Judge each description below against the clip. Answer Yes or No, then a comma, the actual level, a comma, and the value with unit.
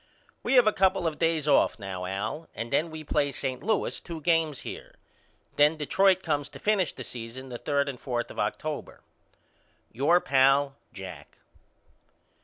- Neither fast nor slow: Yes, average, 165 wpm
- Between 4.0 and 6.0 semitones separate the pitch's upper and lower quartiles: Yes, average, 4.5 semitones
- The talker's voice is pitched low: No, medium, 145 Hz